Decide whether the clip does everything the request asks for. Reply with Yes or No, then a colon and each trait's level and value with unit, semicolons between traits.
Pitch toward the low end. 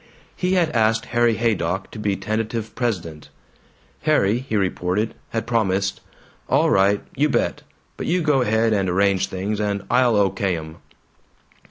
Yes: low, 110 Hz